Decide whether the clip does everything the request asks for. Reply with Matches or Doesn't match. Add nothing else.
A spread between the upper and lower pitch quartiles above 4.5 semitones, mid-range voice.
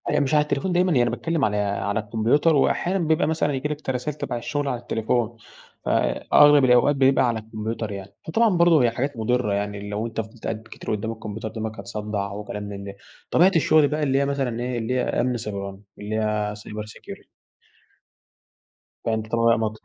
Doesn't match